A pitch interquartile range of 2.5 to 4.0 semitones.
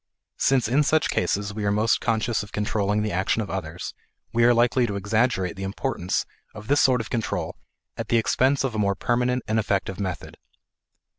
Yes: average, 3.3 semitones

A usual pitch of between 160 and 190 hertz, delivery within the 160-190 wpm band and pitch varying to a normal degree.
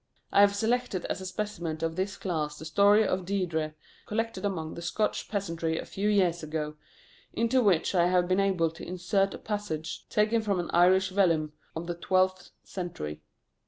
Yes: medium, 185 Hz; average, 180 wpm; average, 3.5 semitones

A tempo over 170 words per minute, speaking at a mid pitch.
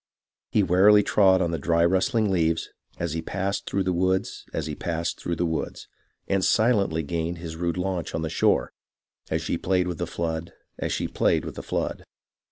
No: average, 195 wpm; very low, 85 Hz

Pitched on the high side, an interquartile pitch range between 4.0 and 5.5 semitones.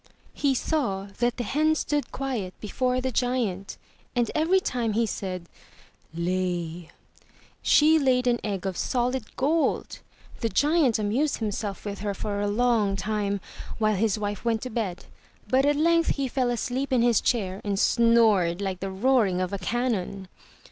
Yes: high, 225 Hz; average, 4.6 semitones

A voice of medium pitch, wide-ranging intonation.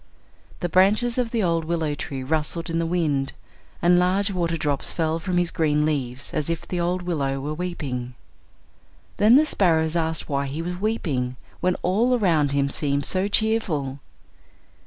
No: medium, 165 Hz; average, 3.9 semitones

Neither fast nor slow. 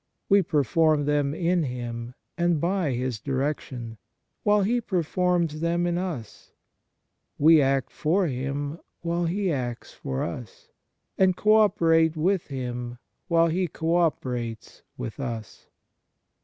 No: slow, 130 wpm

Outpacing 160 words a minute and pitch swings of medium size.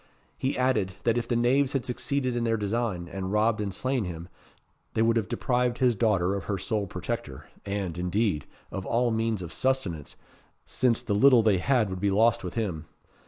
Yes: average, 195 wpm; average, 4.0 semitones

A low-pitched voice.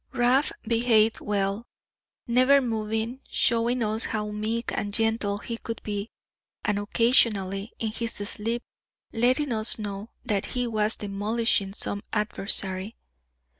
No: high, 220 Hz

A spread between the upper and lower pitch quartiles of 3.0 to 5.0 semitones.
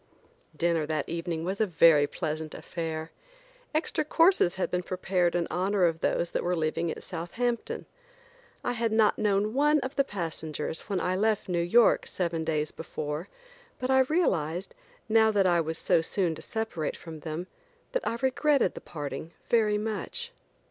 No: wide, 5.4 semitones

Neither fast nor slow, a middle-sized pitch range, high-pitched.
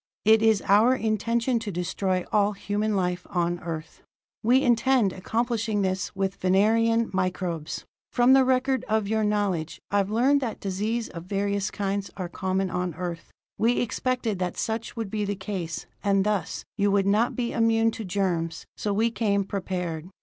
Yes: average, 165 wpm; average, 3.4 semitones; high, 205 Hz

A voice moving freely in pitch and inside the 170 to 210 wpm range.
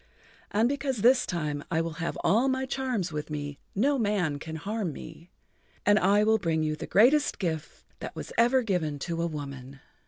Yes: wide, 6.9 semitones; average, 190 wpm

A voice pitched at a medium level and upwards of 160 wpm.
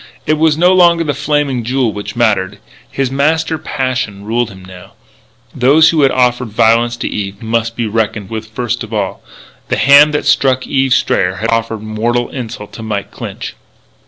No: low, 120 Hz; average, 180 wpm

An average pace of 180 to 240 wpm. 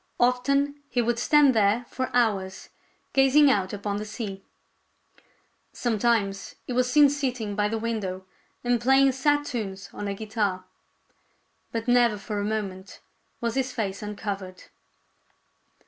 No: slow, 135 wpm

